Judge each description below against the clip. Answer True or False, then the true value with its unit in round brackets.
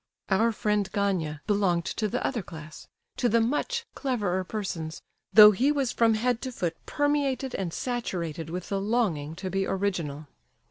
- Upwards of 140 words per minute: True (155 wpm)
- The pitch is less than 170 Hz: False (200 Hz)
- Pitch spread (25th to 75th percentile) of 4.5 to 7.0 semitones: True (5.5 semitones)